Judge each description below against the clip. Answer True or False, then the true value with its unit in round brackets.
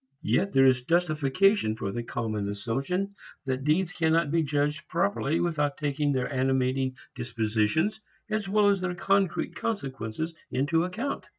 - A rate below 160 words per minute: True (140 wpm)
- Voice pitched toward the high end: False (145 Hz)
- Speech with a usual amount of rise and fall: False (5.7 semitones)